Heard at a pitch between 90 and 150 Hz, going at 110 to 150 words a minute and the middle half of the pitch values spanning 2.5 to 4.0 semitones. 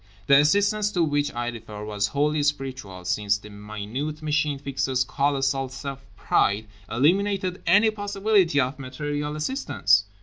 No: medium, 140 Hz; slow, 135 wpm; average, 4.4 semitones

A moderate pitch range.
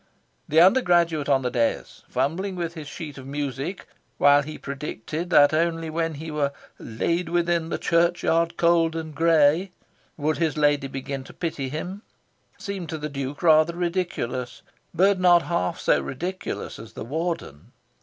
Yes: average, 3.2 semitones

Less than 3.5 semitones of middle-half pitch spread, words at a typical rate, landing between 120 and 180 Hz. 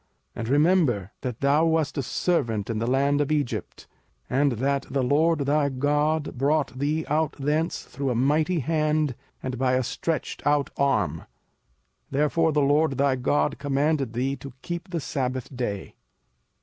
Yes: average, 2.8 semitones; average, 160 wpm; medium, 140 Hz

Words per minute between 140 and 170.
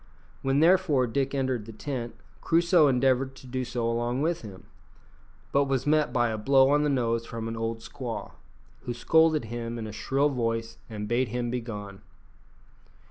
No: average, 180 wpm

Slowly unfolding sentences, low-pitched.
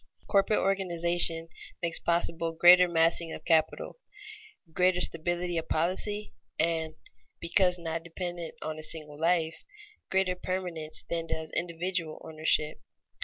No: slow, 120 wpm; medium, 170 Hz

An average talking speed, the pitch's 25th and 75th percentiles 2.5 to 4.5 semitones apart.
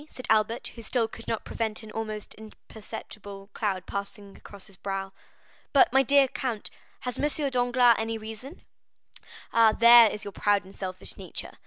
Yes: average, 165 wpm; average, 2.9 semitones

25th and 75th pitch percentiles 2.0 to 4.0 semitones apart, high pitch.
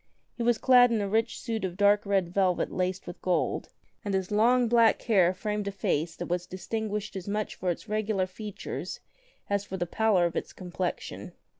Yes: average, 3.0 semitones; high, 200 Hz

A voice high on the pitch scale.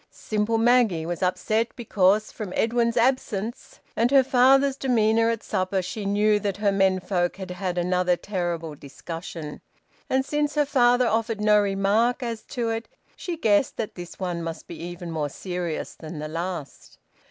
Yes: high, 205 Hz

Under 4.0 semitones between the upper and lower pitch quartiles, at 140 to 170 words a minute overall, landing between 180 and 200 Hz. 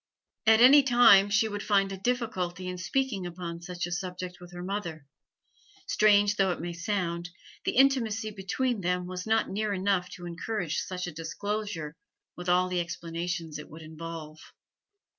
Yes: average, 3.3 semitones; average, 165 wpm; medium, 185 Hz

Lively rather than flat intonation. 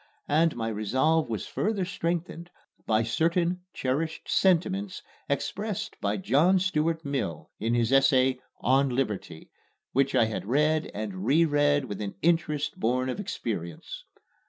Yes: wide, 6.4 semitones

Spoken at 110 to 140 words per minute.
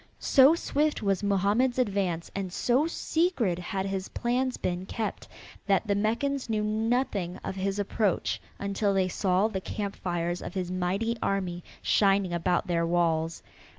No: average, 150 wpm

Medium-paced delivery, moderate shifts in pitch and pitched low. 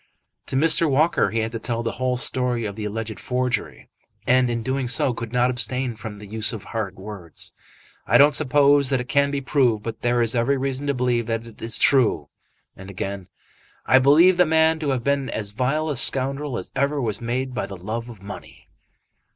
No: fast, 210 wpm; average, 3.6 semitones; low, 125 Hz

